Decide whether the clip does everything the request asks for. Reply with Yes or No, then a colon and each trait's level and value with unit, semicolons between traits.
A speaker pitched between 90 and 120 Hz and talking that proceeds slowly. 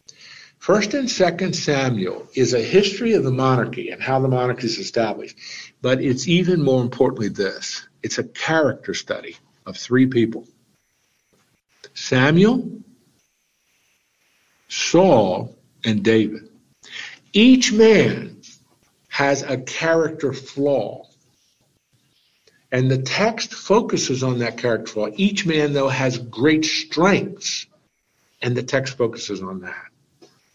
No: low, 135 Hz; slow, 115 wpm